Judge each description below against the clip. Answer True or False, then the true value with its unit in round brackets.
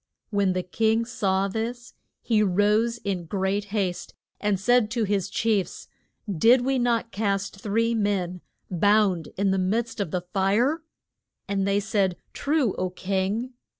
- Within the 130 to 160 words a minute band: True (150 wpm)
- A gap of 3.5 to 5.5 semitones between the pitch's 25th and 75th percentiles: False (3.1 semitones)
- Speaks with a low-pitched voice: False (205 Hz)